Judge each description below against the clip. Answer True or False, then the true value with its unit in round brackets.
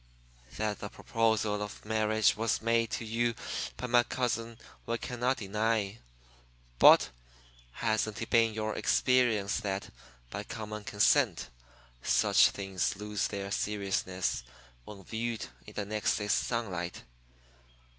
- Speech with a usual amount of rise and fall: False (2.0 semitones)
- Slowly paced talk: True (125 wpm)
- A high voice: False (110 Hz)